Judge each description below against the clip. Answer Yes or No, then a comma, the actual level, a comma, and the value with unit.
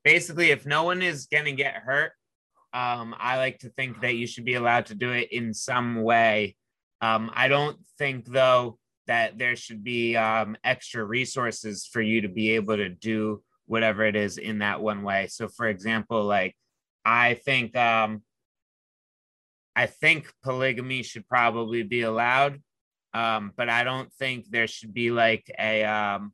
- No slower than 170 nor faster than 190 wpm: Yes, average, 175 wpm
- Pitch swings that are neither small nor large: No, narrow, 2.3 semitones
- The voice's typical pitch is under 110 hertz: No, low, 115 Hz